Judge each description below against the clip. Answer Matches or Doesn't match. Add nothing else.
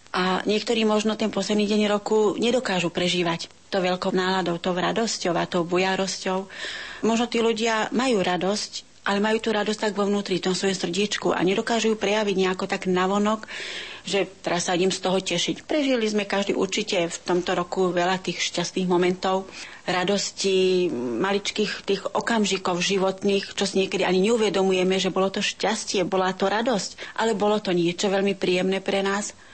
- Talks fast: Matches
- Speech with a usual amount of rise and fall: Doesn't match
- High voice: Matches